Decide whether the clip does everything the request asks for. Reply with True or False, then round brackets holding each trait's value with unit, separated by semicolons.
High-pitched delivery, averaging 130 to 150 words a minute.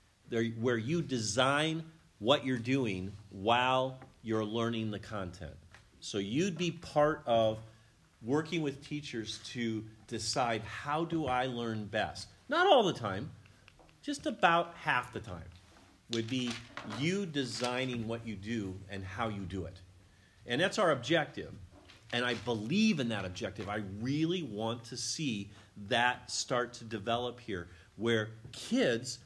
False (115 Hz; 140 wpm)